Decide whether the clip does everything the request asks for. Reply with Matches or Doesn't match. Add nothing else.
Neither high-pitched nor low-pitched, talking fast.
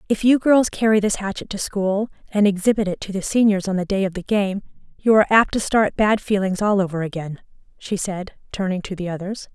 Doesn't match